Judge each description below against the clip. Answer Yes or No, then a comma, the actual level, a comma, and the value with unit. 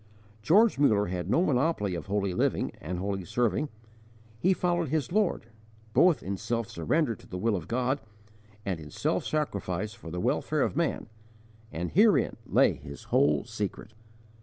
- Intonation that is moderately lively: No, wide, 9.0 semitones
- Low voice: Yes, low, 105 Hz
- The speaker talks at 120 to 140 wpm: No, average, 160 wpm